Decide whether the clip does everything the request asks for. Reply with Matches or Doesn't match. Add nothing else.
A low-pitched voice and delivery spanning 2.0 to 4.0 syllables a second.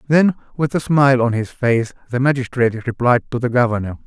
Doesn't match